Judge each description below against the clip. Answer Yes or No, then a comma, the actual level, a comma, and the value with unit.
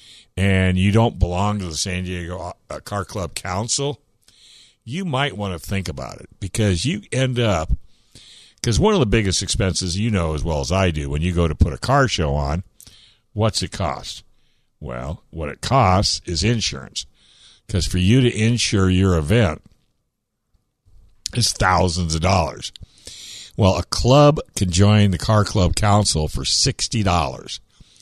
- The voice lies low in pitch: Yes, very low, 95 Hz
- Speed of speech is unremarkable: Yes, average, 160 wpm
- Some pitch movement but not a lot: Yes, average, 4.1 semitones